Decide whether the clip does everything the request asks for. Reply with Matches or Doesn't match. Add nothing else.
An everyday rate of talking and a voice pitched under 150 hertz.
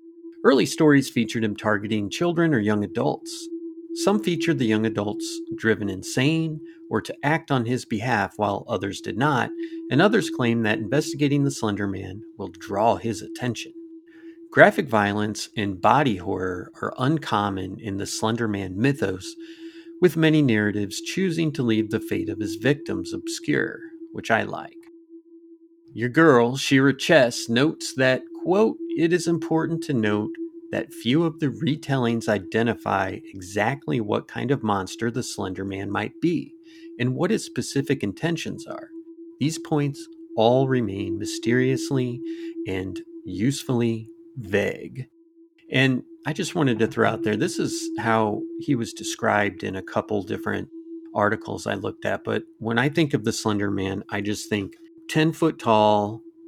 Matches